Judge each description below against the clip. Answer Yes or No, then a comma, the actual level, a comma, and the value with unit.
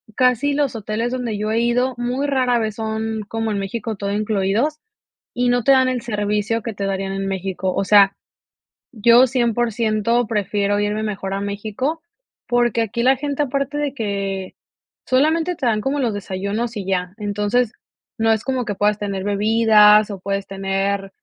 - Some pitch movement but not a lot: Yes, average, 3.4 semitones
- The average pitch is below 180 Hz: No, high, 220 Hz